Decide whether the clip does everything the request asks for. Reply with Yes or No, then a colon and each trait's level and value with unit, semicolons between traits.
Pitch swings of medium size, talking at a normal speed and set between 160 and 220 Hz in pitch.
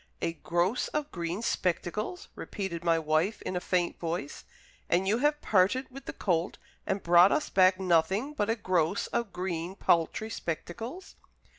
Yes: average, 4.6 semitones; average, 160 wpm; medium, 185 Hz